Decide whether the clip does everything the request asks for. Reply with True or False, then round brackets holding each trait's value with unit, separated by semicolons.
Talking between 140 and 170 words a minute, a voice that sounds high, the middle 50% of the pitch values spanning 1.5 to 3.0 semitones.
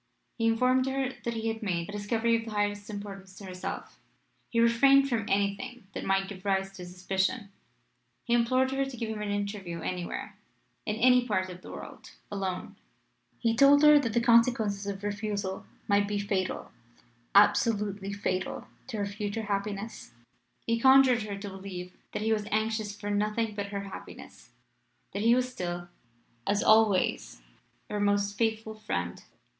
True (165 wpm; 205 Hz; 2.5 semitones)